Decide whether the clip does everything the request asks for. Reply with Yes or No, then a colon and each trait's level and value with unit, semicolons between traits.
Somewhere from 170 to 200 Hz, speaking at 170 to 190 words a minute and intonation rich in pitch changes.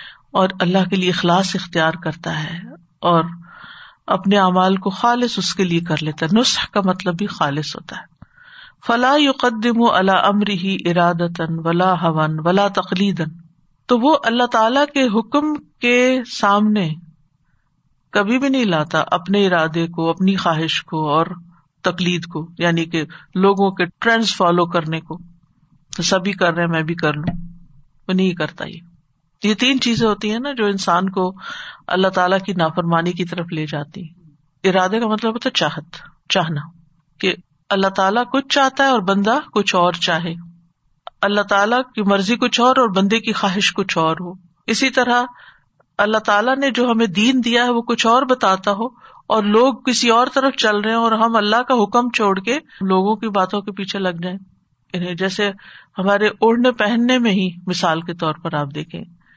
No: high, 190 Hz; average, 175 wpm; average, 4.9 semitones